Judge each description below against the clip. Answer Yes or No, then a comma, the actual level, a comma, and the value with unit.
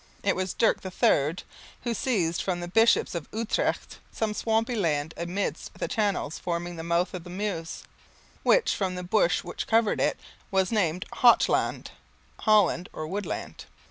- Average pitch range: Yes, average, 3.9 semitones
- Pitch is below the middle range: No, medium, 185 Hz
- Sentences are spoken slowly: No, average, 165 wpm